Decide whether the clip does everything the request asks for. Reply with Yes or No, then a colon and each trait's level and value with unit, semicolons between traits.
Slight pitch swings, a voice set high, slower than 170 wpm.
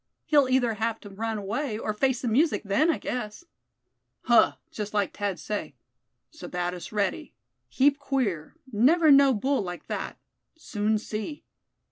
No: average, 5.0 semitones; high, 225 Hz; average, 145 wpm